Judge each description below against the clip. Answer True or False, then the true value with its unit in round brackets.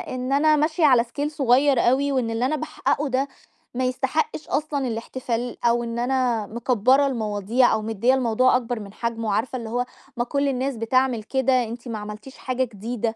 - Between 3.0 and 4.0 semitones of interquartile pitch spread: False (2.6 semitones)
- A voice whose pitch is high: True (250 Hz)